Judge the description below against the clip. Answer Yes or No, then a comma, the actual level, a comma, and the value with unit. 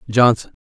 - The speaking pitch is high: No, low, 120 Hz